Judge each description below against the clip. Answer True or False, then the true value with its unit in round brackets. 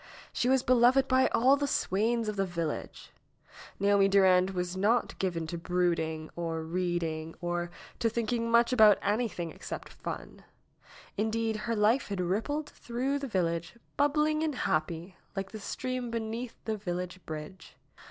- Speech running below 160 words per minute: True (150 wpm)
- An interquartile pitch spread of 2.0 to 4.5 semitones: False (5.4 semitones)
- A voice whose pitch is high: True (205 Hz)